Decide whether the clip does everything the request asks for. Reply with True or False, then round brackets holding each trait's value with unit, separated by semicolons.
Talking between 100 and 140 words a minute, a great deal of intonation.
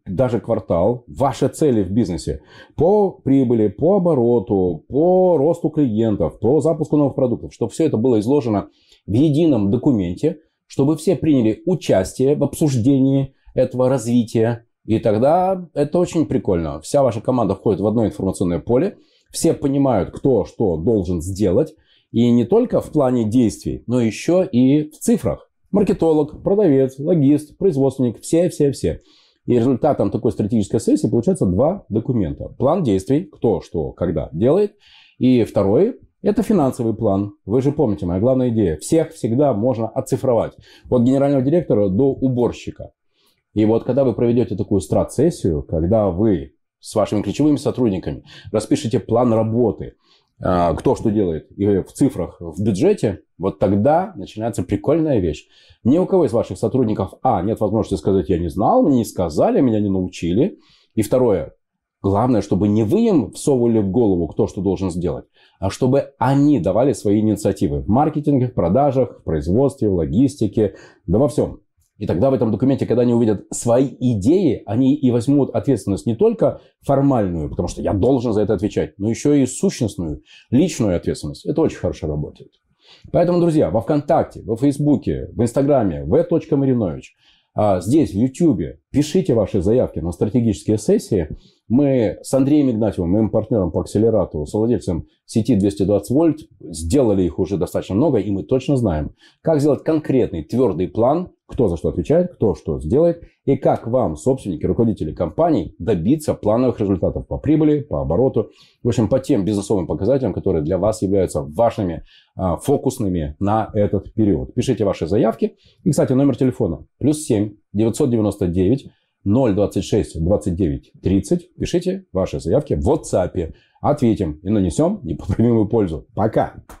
False (150 wpm; 5.7 semitones)